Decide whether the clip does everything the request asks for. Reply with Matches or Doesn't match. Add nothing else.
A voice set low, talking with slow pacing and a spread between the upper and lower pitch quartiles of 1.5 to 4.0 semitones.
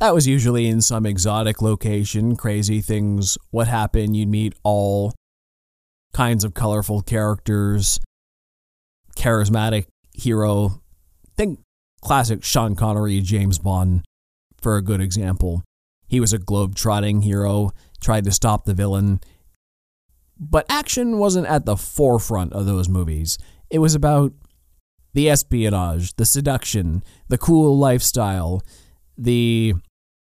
Doesn't match